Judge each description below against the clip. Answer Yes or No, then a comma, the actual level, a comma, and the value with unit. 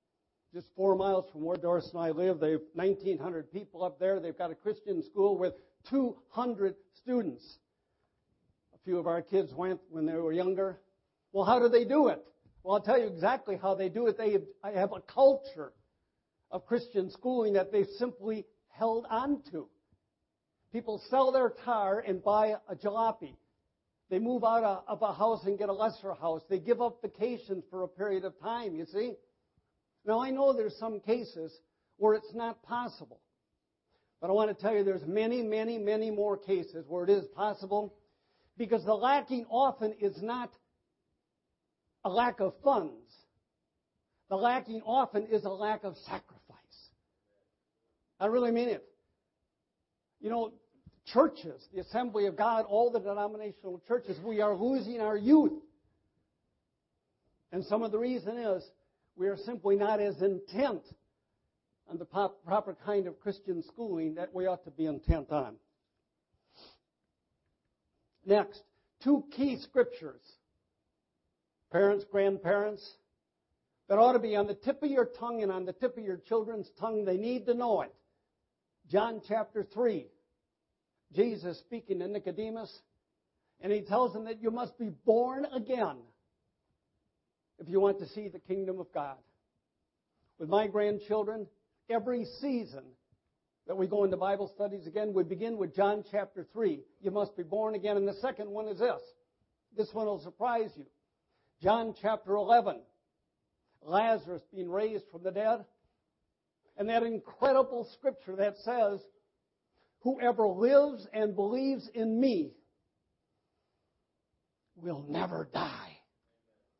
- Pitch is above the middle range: Yes, high, 210 Hz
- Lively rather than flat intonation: No, average, 3.4 semitones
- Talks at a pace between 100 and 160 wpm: Yes, average, 155 wpm